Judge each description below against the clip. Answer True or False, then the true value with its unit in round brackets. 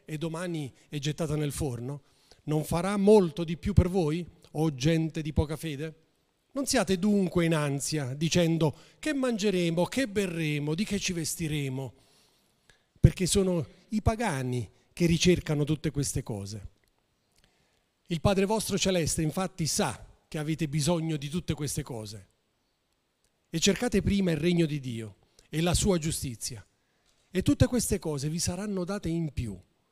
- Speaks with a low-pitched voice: False (160 Hz)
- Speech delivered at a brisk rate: False (150 wpm)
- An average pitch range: True (4.2 semitones)